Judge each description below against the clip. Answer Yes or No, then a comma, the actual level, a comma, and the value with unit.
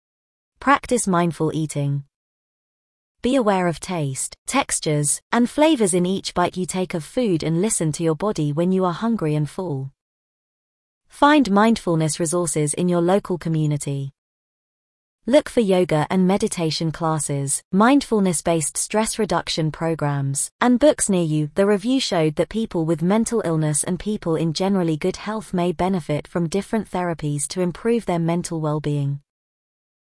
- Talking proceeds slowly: No, average, 150 wpm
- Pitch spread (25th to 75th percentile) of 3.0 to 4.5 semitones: No, average, 4.9 semitones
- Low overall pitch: No, medium, 175 Hz